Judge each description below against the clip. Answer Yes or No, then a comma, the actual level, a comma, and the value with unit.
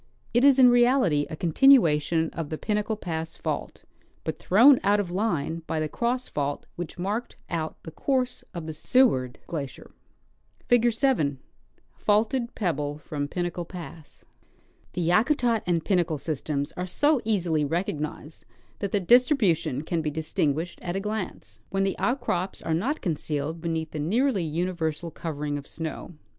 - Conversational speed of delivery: Yes, average, 155 wpm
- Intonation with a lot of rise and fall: Yes, wide, 6.0 semitones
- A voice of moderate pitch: Yes, medium, 175 Hz